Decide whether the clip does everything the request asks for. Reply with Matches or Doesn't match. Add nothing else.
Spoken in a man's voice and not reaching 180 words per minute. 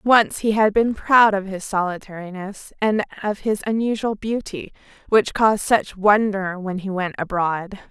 Doesn't match